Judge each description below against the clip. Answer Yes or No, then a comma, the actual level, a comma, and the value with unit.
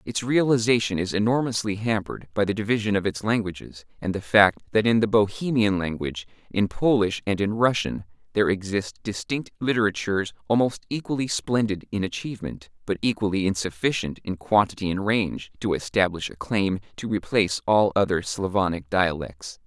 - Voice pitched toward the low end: Yes, low, 100 Hz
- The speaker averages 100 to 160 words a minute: Yes, average, 155 wpm